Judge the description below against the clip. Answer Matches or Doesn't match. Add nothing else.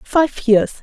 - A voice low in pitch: Doesn't match